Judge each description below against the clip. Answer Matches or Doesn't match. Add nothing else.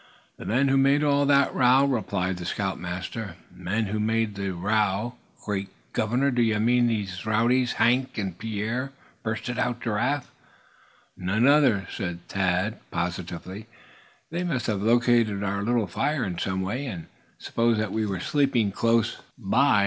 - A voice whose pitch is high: Doesn't match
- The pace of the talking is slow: Doesn't match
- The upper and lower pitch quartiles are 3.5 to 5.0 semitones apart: Matches